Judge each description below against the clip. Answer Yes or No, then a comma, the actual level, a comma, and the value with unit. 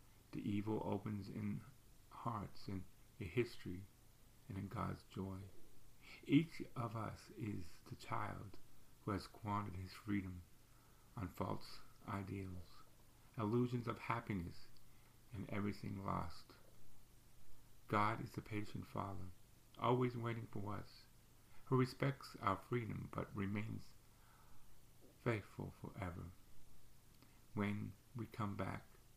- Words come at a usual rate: No, slow, 110 wpm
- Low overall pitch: Yes, low, 110 Hz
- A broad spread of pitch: No, average, 2.9 semitones